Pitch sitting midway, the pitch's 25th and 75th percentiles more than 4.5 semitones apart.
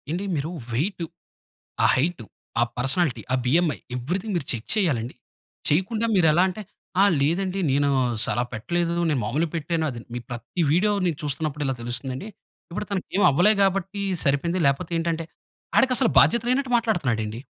Yes: medium, 165 Hz; wide, 5.5 semitones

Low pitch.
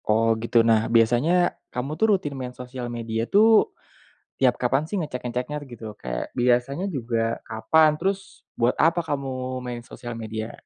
Yes: low, 125 Hz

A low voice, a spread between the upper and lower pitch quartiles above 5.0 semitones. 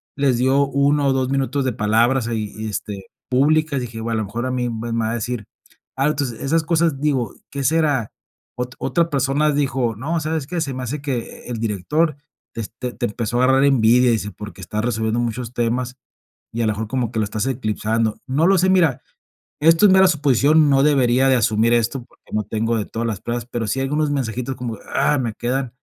No: low, 125 Hz; average, 3.7 semitones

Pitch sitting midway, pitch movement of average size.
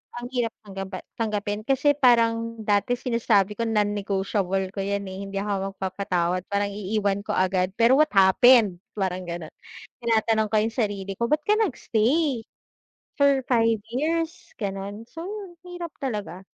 No: high, 210 Hz; average, 3.9 semitones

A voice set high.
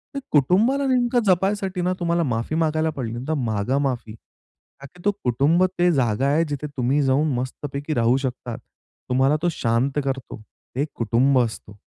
No: medium, 140 Hz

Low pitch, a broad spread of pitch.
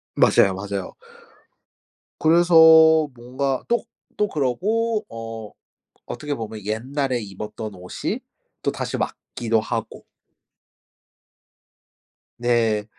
Yes: low, 120 Hz; wide, 6.7 semitones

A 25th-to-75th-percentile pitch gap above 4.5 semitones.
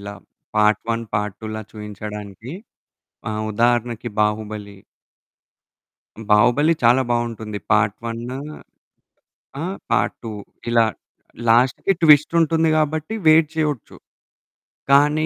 Yes: wide, 5.5 semitones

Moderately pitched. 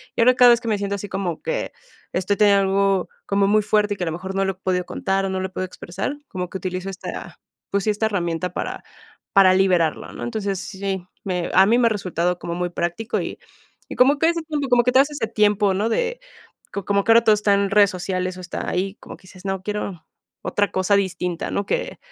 No: high, 195 Hz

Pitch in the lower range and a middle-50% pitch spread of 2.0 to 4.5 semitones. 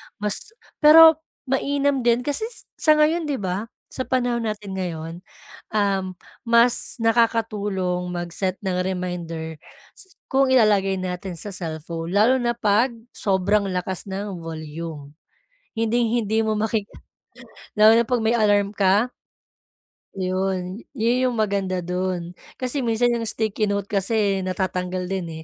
No: high, 205 Hz; average, 4.2 semitones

